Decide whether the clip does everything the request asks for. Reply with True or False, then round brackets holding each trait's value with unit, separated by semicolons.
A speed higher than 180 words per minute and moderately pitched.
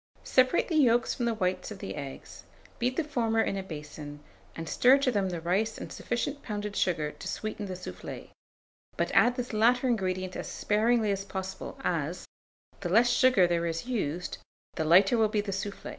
False (190 wpm; 205 Hz)